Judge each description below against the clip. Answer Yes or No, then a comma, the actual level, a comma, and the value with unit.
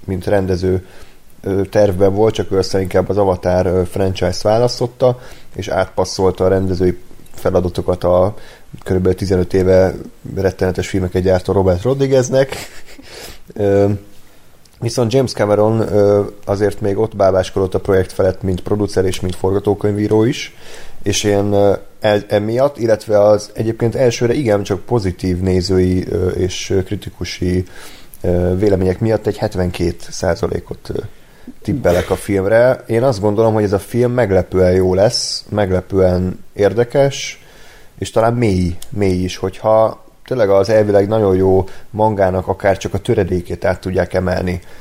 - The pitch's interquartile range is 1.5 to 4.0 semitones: Yes, average, 2.7 semitones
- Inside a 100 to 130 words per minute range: Yes, average, 125 wpm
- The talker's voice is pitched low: Yes, low, 100 Hz